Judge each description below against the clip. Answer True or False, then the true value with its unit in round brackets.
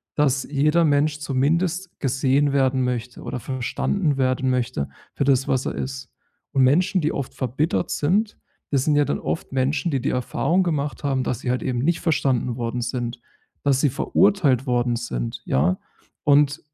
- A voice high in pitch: False (135 Hz)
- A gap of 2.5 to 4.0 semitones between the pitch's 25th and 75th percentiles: True (2.8 semitones)